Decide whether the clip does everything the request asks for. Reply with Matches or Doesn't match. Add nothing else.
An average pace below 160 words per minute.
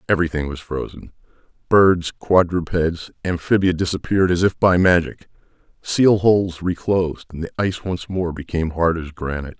Matches